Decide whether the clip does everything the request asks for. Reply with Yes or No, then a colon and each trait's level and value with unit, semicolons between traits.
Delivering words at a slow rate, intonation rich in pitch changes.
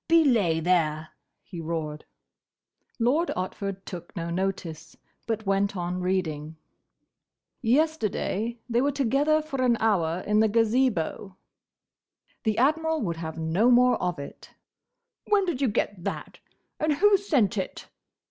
Yes: slow, 130 wpm; wide, 7.0 semitones